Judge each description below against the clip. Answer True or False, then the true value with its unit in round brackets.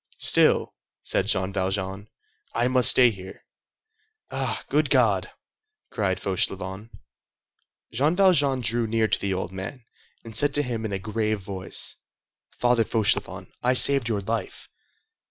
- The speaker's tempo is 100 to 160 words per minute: True (135 wpm)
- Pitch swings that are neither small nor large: True (4.3 semitones)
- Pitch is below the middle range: True (110 Hz)